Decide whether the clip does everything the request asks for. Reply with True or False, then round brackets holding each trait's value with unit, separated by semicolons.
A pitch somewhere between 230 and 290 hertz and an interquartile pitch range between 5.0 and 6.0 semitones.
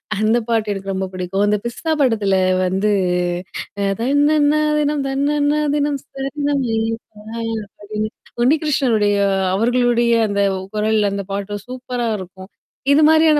True (235 Hz; 5.6 semitones)